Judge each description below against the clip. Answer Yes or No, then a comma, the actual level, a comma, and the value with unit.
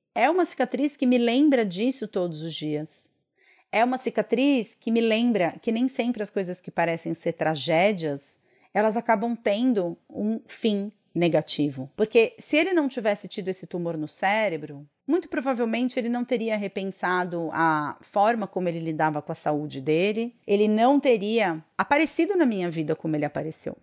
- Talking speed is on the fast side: No, average, 165 wpm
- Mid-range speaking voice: No, high, 210 Hz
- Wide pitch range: Yes, wide, 6.5 semitones